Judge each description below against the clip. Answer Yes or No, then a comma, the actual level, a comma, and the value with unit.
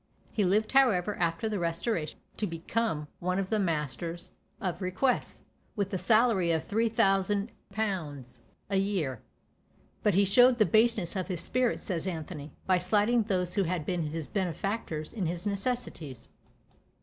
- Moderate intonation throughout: Yes, average, 4.3 semitones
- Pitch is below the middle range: No, high, 190 Hz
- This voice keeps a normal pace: Yes, average, 150 wpm